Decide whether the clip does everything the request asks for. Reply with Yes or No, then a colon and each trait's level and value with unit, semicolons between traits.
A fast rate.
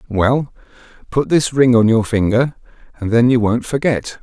No: average, 170 wpm